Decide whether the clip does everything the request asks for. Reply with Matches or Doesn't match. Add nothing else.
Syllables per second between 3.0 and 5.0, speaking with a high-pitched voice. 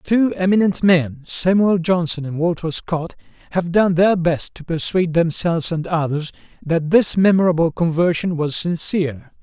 Doesn't match